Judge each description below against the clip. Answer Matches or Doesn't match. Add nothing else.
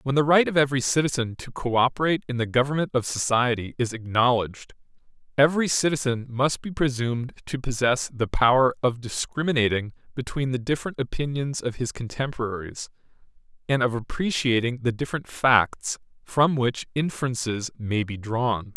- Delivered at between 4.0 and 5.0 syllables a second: Doesn't match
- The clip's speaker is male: Matches